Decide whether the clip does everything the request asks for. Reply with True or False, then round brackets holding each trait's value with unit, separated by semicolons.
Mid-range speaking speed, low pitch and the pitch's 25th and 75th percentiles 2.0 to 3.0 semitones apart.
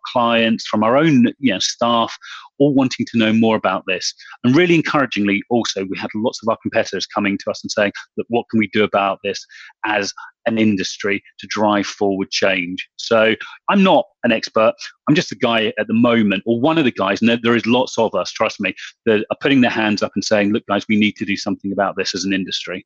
False (230 wpm; 110 Hz; 2.7 semitones)